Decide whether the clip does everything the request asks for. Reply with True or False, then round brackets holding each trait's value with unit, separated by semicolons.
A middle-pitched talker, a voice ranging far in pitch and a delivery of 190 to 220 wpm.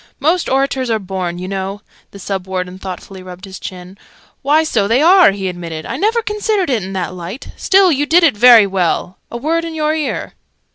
False (205 Hz; 8.8 semitones; 205 wpm)